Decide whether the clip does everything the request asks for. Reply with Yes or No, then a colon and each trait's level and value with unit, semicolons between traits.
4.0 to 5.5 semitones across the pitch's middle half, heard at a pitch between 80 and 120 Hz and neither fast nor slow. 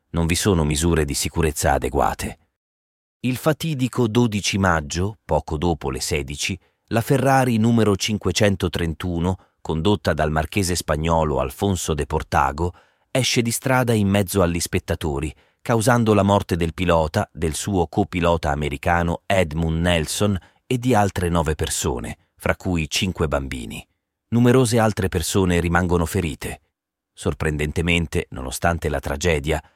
Yes: average, 4.4 semitones; very low, 85 Hz; average, 125 wpm